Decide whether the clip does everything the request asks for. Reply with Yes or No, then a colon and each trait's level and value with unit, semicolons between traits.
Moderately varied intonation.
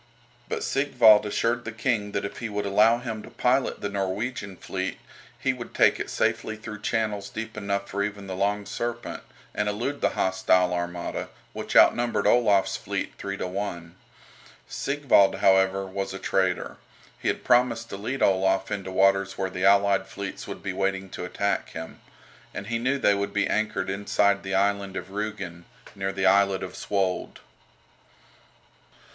No: narrow, 2.1 semitones